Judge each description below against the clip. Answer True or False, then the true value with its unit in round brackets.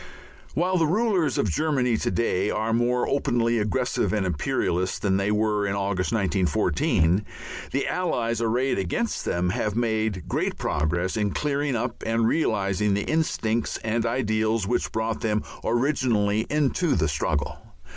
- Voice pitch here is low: True (110 Hz)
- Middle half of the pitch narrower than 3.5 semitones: False (4.0 semitones)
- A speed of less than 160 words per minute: True (145 wpm)